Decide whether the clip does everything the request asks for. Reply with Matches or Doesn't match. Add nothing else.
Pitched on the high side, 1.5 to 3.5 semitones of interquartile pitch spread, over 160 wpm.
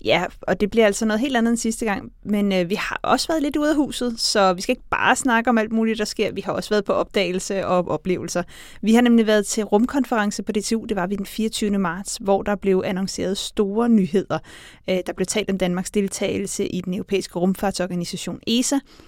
Matches